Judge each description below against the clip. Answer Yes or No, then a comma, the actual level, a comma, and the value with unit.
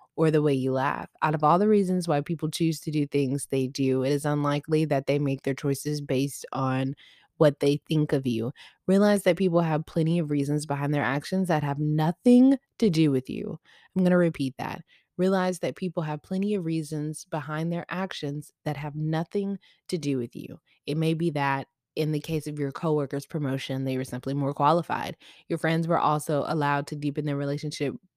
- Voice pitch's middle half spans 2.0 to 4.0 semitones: Yes, average, 3.0 semitones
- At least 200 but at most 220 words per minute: Yes, fast, 205 wpm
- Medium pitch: Yes, medium, 150 Hz